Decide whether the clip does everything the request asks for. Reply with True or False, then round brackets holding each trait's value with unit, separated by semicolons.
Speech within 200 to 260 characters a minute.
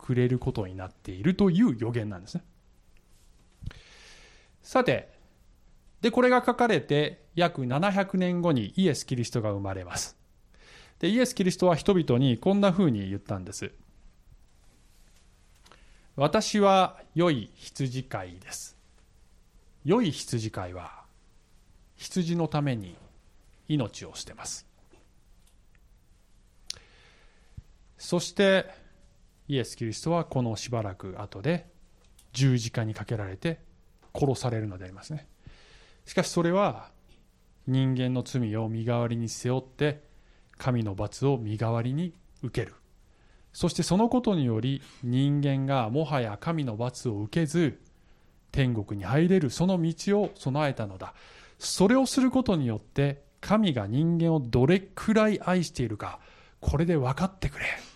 True (250 characters per minute)